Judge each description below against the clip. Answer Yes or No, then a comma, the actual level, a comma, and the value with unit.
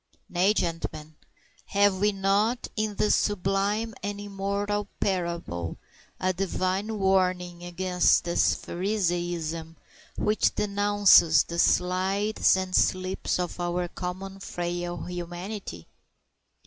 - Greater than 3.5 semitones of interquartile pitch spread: No, narrow, 2.6 semitones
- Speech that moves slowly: Yes, slow, 100 wpm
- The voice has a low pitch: No, medium, 185 Hz